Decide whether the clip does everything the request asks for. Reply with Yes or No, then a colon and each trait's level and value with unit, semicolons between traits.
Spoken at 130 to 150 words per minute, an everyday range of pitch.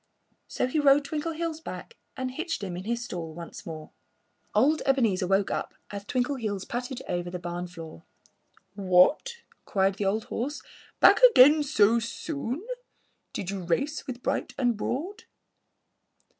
No: average, 145 wpm; wide, 7.3 semitones